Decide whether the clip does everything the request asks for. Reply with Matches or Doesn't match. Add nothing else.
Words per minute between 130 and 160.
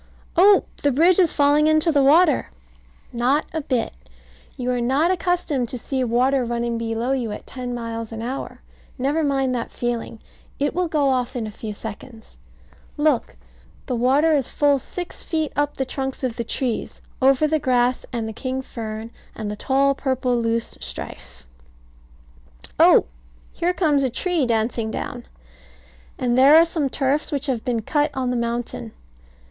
Doesn't match